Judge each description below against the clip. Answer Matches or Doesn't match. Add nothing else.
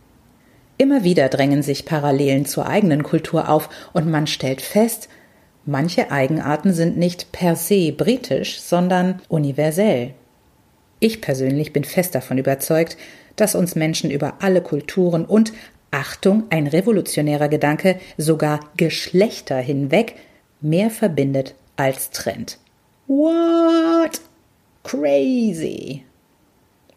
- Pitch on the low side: Doesn't match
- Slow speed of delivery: Matches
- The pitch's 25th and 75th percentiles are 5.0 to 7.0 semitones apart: Matches